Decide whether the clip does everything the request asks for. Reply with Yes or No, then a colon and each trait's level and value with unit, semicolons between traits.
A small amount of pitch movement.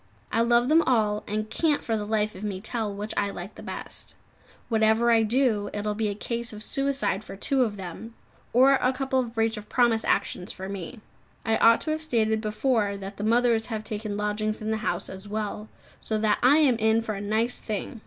Yes: narrow, 2.3 semitones